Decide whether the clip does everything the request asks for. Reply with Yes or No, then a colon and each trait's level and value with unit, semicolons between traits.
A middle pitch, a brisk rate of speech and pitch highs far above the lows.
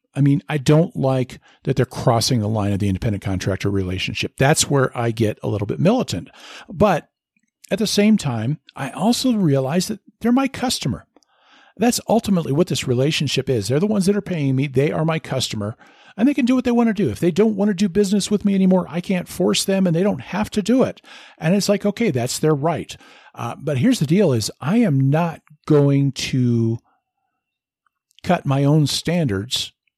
Yes: medium, 160 Hz; fast, 210 wpm; wide, 7.6 semitones